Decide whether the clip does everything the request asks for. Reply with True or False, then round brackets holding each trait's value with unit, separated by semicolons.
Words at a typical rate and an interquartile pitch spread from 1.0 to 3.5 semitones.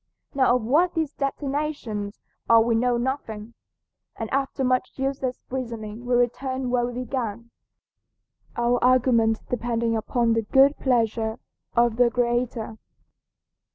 False (125 wpm; 2.4 semitones)